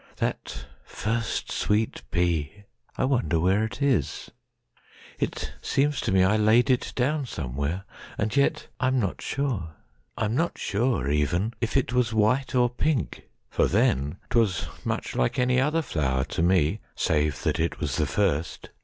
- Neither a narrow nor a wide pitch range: No, wide, 7.6 semitones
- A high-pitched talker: No, low, 105 Hz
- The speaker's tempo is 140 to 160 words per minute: Yes, average, 145 wpm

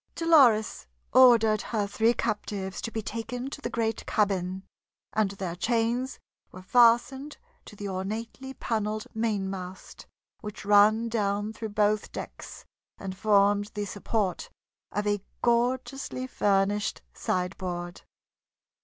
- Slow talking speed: Yes, slow, 120 wpm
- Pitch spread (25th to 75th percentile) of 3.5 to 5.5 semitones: No, average, 2.7 semitones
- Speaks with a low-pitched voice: No, high, 210 Hz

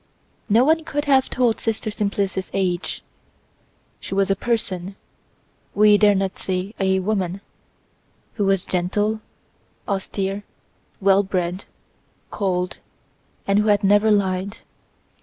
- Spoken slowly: Yes, slow, 110 wpm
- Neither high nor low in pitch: No, high, 200 Hz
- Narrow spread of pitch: Yes, narrow, 2.0 semitones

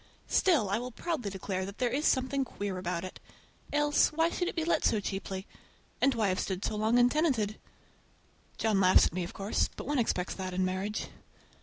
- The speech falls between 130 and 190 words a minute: No, average, 200 wpm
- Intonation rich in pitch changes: Yes, wide, 6.1 semitones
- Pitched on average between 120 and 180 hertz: No, high, 215 Hz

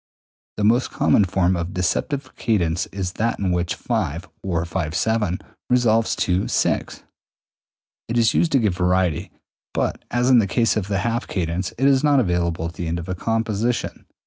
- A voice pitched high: No, very low, 95 Hz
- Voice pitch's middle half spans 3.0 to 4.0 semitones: No, average, 4.8 semitones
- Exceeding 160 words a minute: Yes, average, 170 wpm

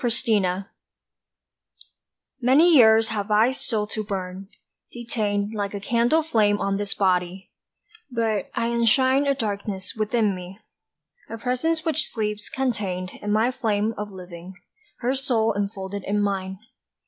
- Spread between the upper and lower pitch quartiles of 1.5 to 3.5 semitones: Yes, average, 3.1 semitones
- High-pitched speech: Yes, high, 210 Hz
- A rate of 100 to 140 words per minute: Yes, slow, 135 wpm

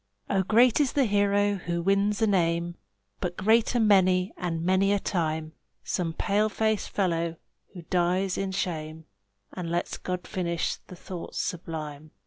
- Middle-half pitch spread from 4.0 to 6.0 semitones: No, average, 3.0 semitones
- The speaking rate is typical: Yes, average, 150 wpm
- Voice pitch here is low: No, medium, 185 Hz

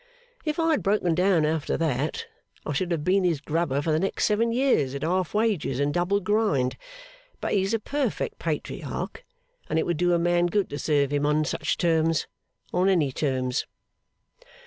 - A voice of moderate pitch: Yes, medium, 170 Hz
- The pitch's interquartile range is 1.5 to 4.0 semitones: No, average, 4.9 semitones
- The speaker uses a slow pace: No, average, 185 wpm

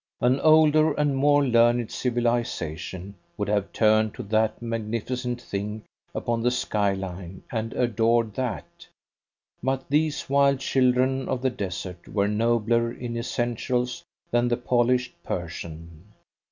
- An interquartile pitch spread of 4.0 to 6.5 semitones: No, average, 3.3 semitones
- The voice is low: Yes, low, 120 Hz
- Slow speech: Yes, slow, 125 wpm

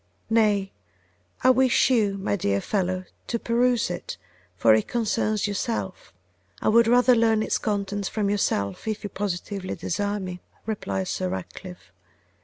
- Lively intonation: No, average, 3.5 semitones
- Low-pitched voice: No, high, 205 Hz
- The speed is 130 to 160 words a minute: Yes, average, 145 wpm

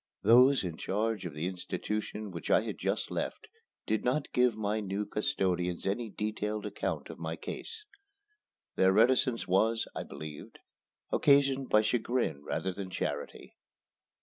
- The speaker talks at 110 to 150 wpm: Yes, average, 145 wpm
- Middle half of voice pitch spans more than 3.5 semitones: Yes, average, 4.3 semitones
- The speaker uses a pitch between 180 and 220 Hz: No, low, 105 Hz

